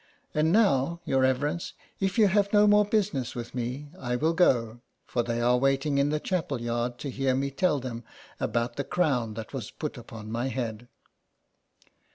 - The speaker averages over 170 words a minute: Yes, average, 185 wpm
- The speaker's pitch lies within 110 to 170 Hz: Yes, low, 135 Hz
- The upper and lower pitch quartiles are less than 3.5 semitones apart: No, average, 5.1 semitones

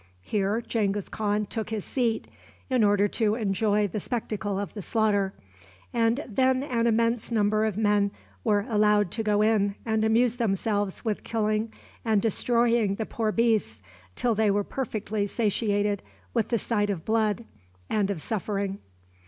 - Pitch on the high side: Yes, high, 215 Hz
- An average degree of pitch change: No, narrow, 1.9 semitones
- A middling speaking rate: Yes, average, 155 wpm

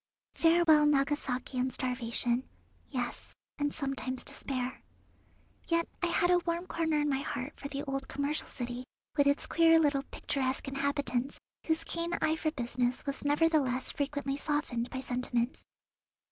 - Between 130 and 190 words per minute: Yes, average, 145 wpm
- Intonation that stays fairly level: No, average, 3.3 semitones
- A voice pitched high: Yes, very high, 280 Hz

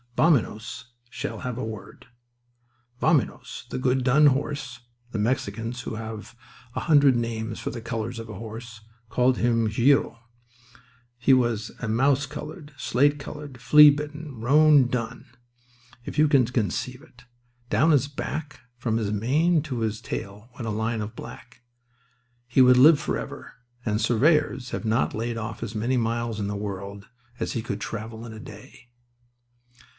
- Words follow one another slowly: No, average, 155 wpm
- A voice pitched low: Yes, low, 120 Hz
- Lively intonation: No, average, 3.4 semitones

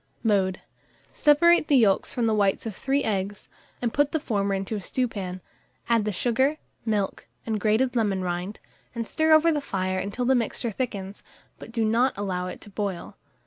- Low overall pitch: No, high, 215 Hz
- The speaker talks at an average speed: Yes, average, 185 wpm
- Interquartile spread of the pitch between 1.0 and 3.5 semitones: No, average, 4.5 semitones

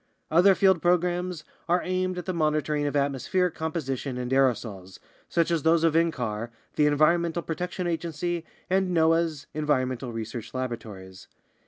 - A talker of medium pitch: Yes, medium, 155 Hz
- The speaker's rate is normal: Yes, average, 150 wpm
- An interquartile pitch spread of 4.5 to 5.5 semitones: Yes, average, 5.1 semitones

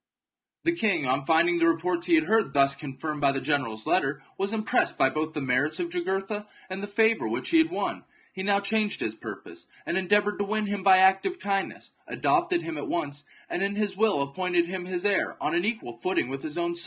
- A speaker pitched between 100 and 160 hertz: No, medium, 185 Hz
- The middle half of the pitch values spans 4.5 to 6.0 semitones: Yes, wide, 5.5 semitones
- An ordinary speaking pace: No, fast, 225 wpm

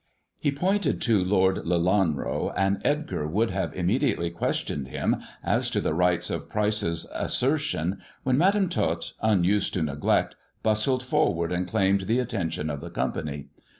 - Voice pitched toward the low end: Yes, very low, 95 Hz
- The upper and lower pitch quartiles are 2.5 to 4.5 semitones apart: No, wide, 5.6 semitones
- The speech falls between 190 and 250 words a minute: No, average, 155 wpm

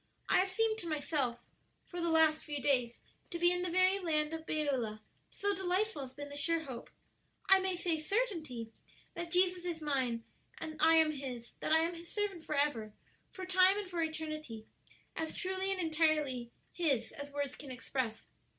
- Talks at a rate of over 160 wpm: Yes, average, 185 wpm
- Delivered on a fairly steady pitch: No, average, 4.3 semitones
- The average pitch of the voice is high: Yes, very high, 315 Hz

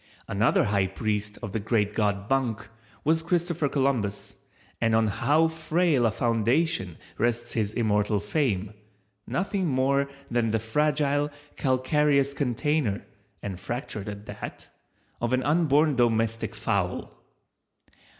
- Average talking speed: No, slow, 120 wpm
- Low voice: Yes, low, 120 Hz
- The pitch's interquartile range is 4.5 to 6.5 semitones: Yes, wide, 5.5 semitones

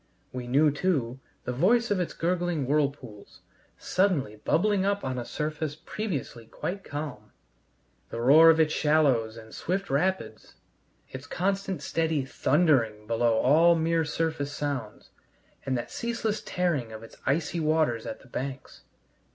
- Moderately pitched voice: Yes, medium, 150 Hz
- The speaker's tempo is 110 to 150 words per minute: Yes, average, 145 wpm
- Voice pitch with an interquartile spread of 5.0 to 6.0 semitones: Yes, wide, 5.6 semitones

